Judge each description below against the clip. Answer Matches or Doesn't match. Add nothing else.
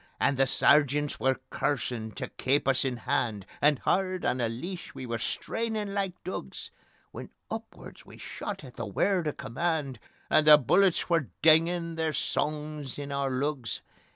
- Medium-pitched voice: Matches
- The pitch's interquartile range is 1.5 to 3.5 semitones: Doesn't match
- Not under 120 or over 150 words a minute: Doesn't match